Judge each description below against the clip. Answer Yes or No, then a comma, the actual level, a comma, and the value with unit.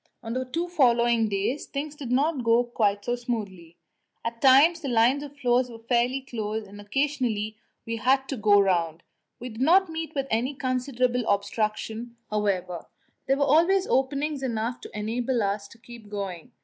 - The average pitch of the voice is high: Yes, high, 240 Hz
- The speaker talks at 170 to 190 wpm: Yes, average, 175 wpm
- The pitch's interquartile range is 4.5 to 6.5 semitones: No, average, 4.1 semitones